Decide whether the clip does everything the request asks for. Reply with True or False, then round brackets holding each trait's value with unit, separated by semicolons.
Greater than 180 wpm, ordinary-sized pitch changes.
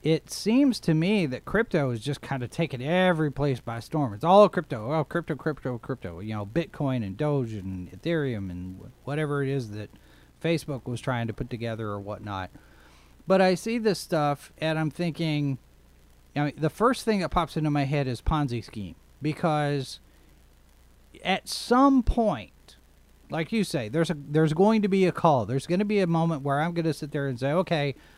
False (200 wpm; 6.5 semitones)